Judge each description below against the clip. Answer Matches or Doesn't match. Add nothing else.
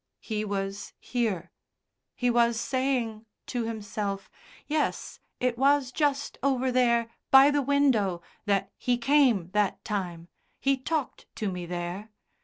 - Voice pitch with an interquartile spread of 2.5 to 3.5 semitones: Doesn't match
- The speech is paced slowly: Matches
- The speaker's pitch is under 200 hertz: Doesn't match